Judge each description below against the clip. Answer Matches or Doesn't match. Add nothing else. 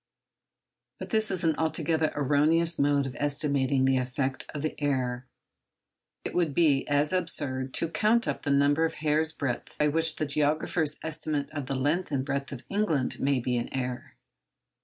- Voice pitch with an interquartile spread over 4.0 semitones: Doesn't match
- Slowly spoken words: Doesn't match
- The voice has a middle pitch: Matches